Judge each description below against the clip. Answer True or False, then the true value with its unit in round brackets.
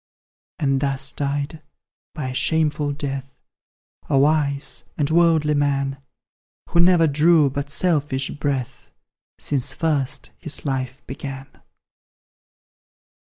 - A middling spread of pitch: False (2.0 semitones)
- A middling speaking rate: False (105 wpm)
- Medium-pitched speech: True (145 Hz)